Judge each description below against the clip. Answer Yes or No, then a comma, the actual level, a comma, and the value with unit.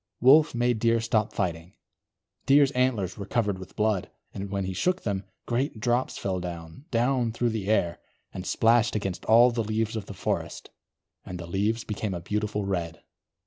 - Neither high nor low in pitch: No, low, 110 Hz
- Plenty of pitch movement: No, average, 3.8 semitones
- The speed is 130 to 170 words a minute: No, average, 180 wpm